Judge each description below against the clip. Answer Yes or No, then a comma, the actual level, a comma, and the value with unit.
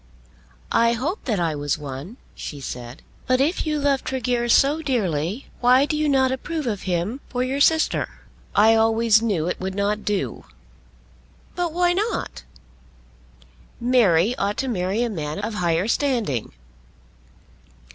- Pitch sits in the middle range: No, high, 230 Hz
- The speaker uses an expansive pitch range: Yes, wide, 6.5 semitones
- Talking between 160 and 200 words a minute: No, average, 145 wpm